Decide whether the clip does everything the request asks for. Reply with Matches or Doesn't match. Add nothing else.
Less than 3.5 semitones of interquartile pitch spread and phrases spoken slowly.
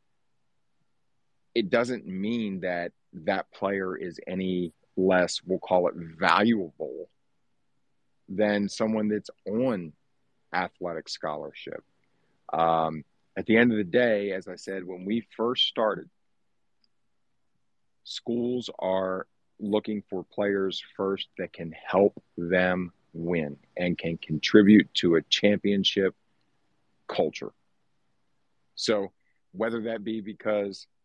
Matches